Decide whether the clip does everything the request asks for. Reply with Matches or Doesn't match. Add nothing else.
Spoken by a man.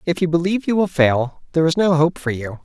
Matches